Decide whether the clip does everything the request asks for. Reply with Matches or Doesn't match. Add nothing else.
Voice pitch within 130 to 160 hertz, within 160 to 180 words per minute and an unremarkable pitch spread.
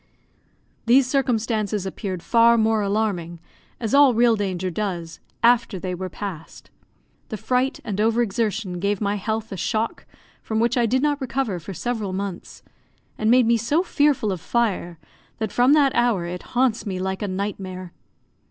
Doesn't match